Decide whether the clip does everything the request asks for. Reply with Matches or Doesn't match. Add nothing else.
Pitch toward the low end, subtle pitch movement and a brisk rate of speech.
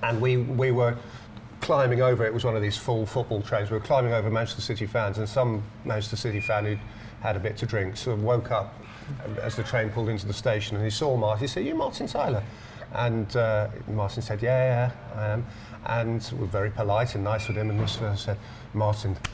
Matches